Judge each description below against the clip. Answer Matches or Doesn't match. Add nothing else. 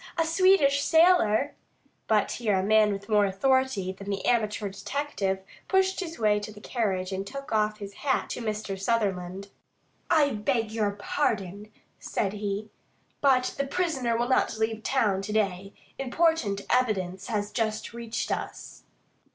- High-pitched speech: Matches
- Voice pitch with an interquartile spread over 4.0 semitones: Matches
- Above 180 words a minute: Doesn't match